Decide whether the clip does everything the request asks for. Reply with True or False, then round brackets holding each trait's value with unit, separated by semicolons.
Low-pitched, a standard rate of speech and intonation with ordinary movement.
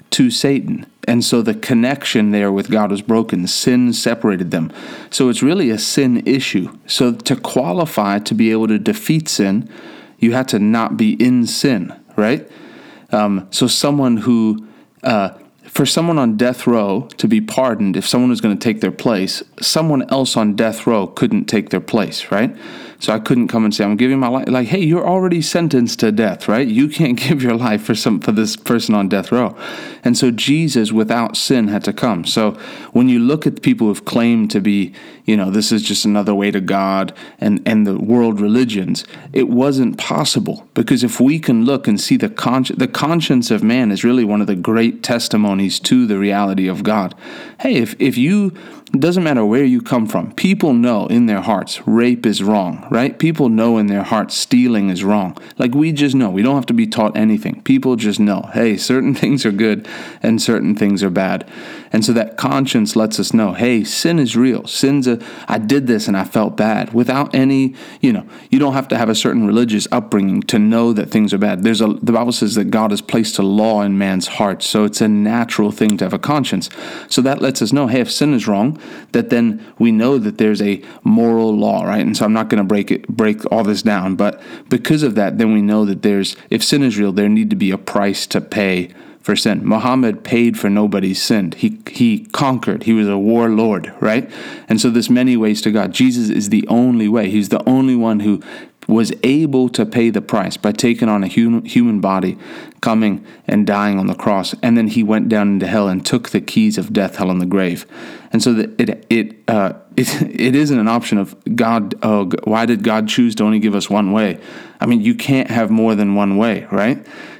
False (115 Hz; 220 wpm; 4.3 semitones)